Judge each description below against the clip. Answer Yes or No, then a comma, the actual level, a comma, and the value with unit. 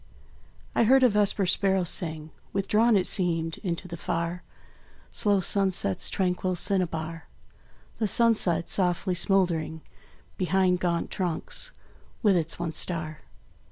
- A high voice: No, medium, 180 Hz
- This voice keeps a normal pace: No, slow, 120 wpm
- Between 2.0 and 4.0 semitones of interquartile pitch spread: Yes, average, 2.8 semitones